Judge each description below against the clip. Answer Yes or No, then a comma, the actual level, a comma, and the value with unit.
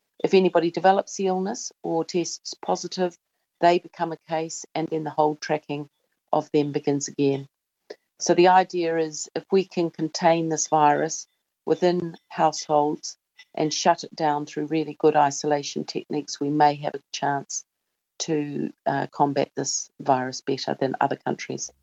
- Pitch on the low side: No, medium, 160 Hz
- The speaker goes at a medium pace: Yes, average, 155 wpm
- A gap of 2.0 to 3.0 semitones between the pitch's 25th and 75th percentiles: Yes, narrow, 2.5 semitones